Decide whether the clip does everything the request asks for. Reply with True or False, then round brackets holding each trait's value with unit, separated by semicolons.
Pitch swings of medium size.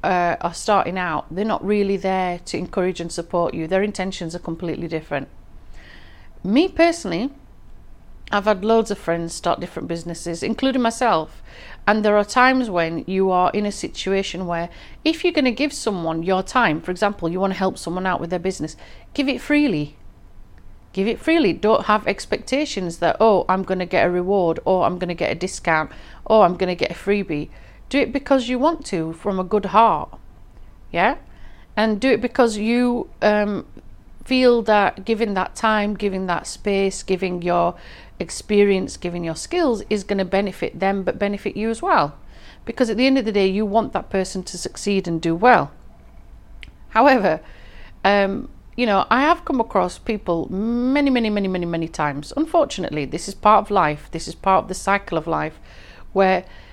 True (4.5 semitones)